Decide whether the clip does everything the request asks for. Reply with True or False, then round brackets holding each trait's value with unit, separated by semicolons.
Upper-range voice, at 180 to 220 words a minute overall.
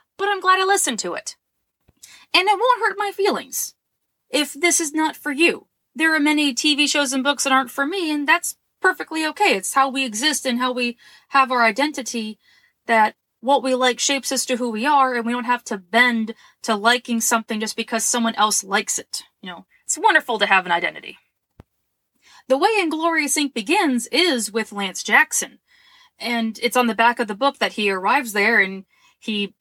True (260 Hz; 205 wpm)